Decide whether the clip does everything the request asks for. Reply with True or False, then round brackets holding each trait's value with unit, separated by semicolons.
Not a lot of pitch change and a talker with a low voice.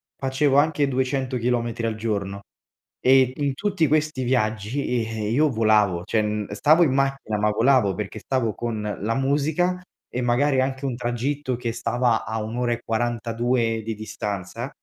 False (3.6 semitones; 120 Hz)